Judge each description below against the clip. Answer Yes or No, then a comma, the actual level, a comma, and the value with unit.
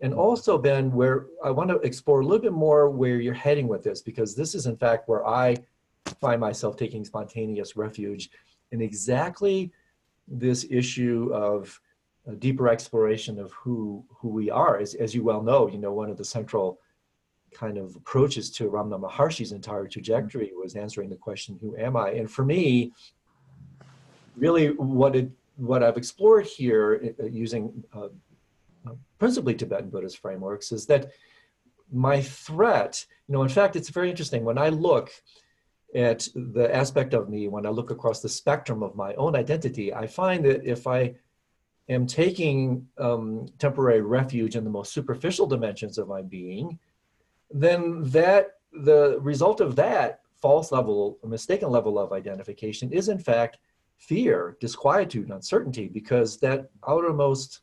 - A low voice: Yes, low, 125 Hz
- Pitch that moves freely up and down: No, average, 4.5 semitones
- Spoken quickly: No, average, 160 wpm